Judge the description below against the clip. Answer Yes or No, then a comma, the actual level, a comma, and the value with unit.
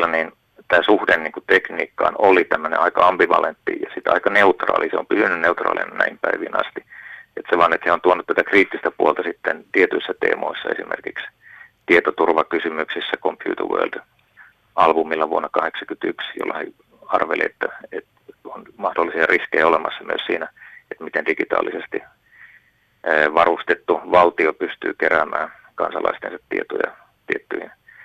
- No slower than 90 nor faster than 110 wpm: No, average, 130 wpm